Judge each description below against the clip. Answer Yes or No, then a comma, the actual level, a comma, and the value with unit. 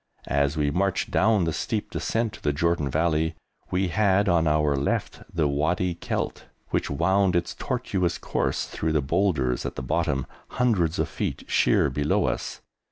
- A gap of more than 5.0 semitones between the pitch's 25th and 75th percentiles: No, average, 4.4 semitones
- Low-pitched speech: Yes, very low, 85 Hz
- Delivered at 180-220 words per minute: No, average, 165 wpm